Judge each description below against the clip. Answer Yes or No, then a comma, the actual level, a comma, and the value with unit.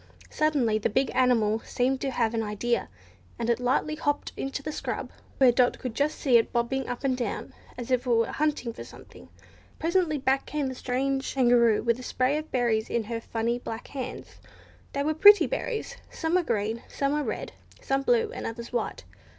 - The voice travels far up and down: No, average, 3.4 semitones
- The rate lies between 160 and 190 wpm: No, average, 200 wpm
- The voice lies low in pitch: No, very high, 255 Hz